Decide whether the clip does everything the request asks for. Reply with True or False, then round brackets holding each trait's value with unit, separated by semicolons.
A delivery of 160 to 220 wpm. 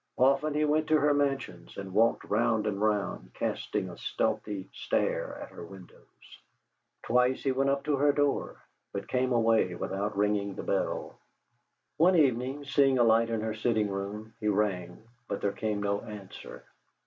True (170 wpm)